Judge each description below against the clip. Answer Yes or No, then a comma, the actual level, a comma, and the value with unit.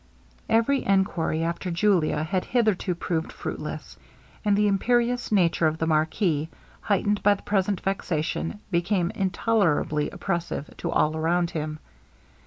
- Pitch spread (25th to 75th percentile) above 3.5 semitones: Yes, average, 4.2 semitones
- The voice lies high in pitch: No, medium, 180 Hz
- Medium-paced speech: No, slow, 130 wpm